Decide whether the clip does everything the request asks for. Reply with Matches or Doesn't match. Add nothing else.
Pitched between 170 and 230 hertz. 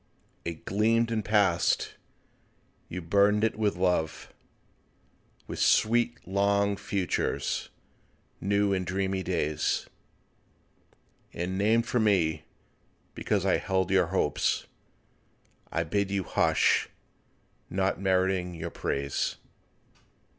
Doesn't match